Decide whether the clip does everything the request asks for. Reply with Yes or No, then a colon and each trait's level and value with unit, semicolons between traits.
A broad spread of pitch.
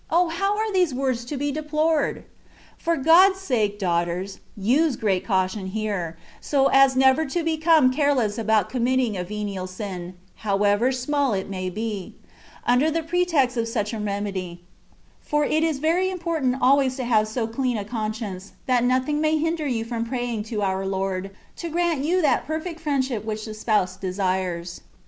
Yes: wide, 6.8 semitones